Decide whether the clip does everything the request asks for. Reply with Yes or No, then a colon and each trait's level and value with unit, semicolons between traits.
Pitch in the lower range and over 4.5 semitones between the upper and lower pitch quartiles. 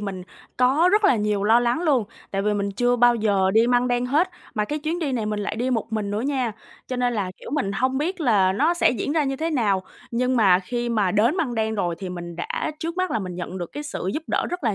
No: high, 235 Hz; average, 5.2 semitones